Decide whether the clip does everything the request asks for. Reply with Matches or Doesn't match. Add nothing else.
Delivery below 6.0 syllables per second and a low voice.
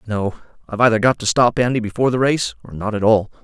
Doesn't match